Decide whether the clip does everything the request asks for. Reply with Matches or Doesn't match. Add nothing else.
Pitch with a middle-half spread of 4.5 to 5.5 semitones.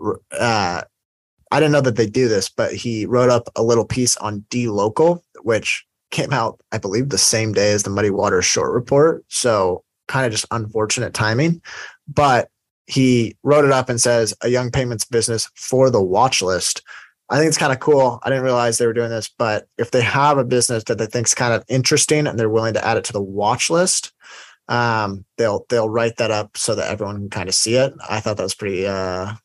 Doesn't match